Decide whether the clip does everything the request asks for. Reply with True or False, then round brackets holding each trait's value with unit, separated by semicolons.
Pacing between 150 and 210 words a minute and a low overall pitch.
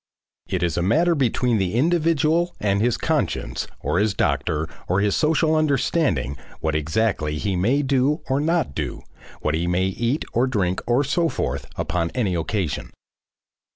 True (160 wpm; 110 Hz)